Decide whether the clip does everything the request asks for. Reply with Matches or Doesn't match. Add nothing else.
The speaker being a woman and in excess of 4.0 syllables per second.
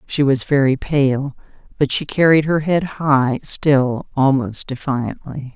Doesn't match